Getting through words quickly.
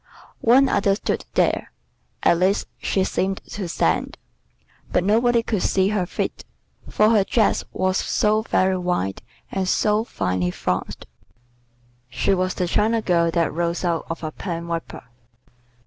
No: average, 150 wpm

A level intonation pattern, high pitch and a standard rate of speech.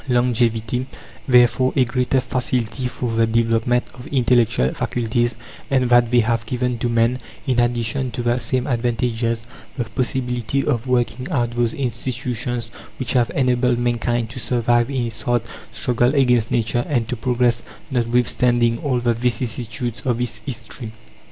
No: narrow, 1.3 semitones; low, 120 Hz; average, 150 wpm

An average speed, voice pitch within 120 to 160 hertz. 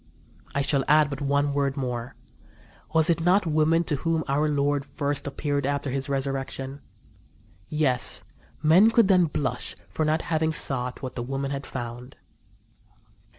Yes: average, 150 wpm; medium, 140 Hz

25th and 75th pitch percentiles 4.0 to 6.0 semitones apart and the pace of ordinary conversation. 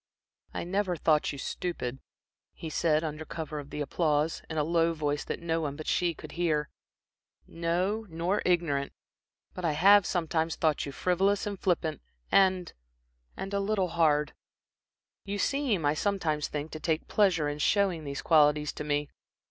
No: average, 3.3 semitones; average, 165 wpm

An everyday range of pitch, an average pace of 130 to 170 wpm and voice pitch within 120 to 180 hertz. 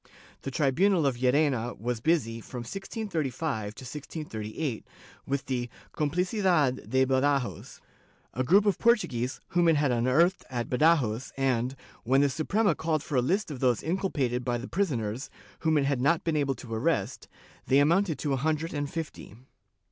Yes: average, 4.7 semitones; average, 165 wpm; medium, 140 Hz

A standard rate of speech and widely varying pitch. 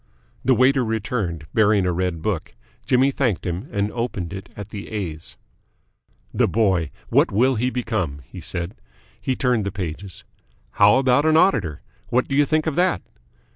Yes: average, 170 wpm; wide, 5.7 semitones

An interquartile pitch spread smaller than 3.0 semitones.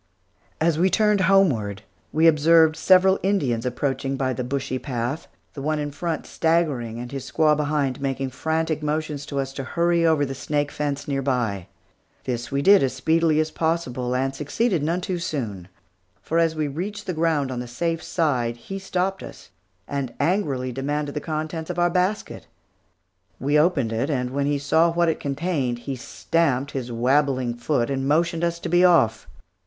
No: average, 4.1 semitones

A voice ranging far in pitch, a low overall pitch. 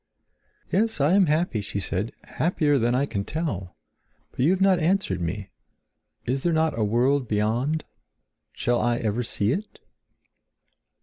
Yes: wide, 7.1 semitones; low, 130 Hz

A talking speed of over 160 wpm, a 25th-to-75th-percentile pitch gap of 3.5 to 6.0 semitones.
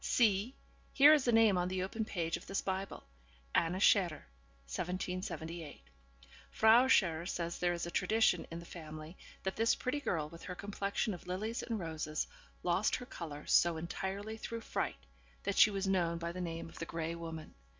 Yes: average, 180 wpm; average, 3.8 semitones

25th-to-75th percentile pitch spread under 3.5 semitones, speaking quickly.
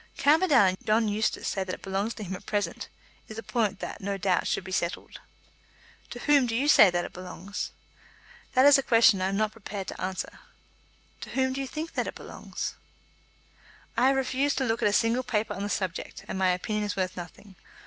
No: average, 5.0 semitones; fast, 220 wpm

